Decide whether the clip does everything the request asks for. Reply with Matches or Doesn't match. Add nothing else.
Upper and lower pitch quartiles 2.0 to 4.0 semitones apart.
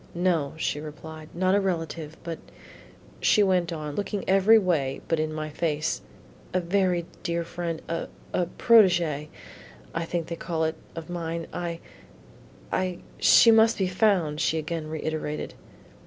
Matches